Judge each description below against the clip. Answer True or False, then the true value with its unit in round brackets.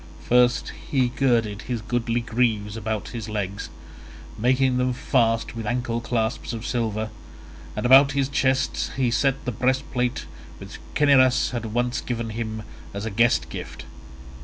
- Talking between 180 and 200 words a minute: False (145 wpm)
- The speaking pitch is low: True (120 Hz)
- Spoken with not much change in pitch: True (2.3 semitones)